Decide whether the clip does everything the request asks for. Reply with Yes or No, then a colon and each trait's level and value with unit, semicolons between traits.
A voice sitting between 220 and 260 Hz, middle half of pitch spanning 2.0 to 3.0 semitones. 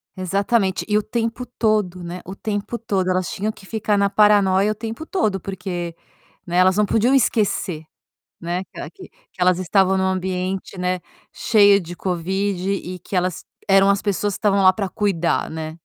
No: high, 195 Hz; narrow, 2.4 semitones